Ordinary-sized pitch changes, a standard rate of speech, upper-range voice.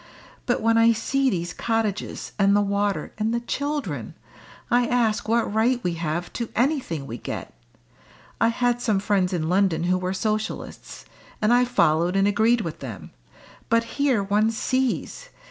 Yes: average, 4.3 semitones; average, 165 wpm; high, 215 Hz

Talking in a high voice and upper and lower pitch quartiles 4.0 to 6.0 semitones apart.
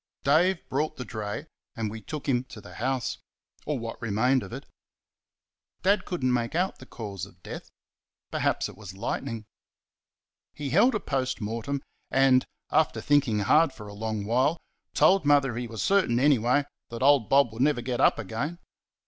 No: low, 130 Hz; average, 4.4 semitones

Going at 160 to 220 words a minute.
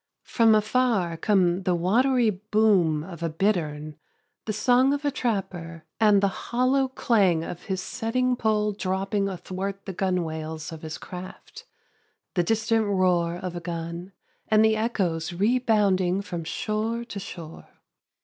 No: average, 140 wpm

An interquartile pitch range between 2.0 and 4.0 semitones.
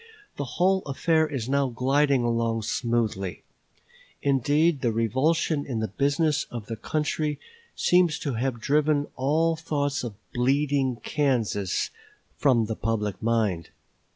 No: average, 4.4 semitones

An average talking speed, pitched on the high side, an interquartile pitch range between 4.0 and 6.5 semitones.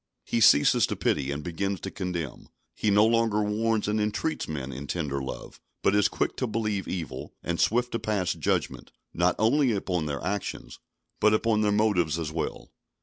No: average, 185 wpm; low, 100 Hz; average, 4.9 semitones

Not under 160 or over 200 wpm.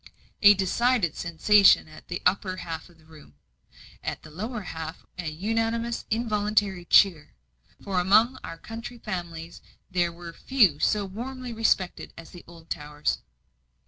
No: average, 140 wpm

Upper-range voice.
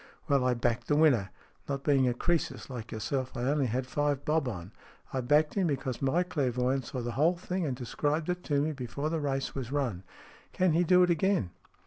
No: medium, 140 Hz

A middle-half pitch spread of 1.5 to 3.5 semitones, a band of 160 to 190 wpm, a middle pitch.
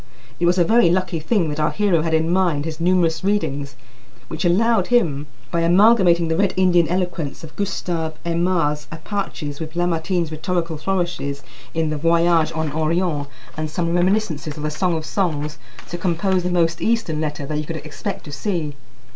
Yes: average, 2.8 semitones; average, 180 wpm; medium, 170 Hz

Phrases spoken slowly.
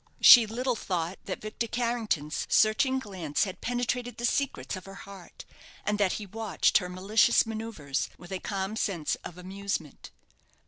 No: average, 155 wpm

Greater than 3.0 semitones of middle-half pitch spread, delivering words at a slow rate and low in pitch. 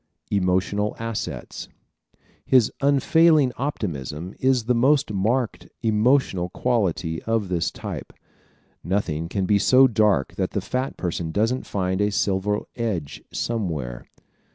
Yes: average, 5.3 semitones; slow, 125 wpm; low, 105 Hz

